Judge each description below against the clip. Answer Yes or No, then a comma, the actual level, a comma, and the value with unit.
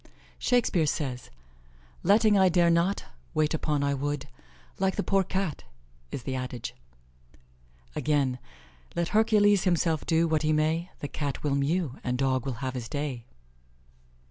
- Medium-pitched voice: Yes, medium, 155 Hz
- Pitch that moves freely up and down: No, average, 5.0 semitones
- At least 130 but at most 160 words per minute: Yes, average, 145 wpm